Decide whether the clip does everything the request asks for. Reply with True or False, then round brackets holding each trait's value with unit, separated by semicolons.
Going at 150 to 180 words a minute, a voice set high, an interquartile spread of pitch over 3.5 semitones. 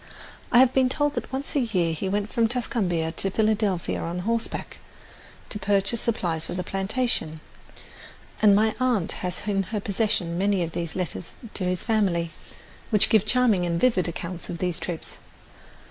True (170 wpm; 195 Hz; 4.4 semitones)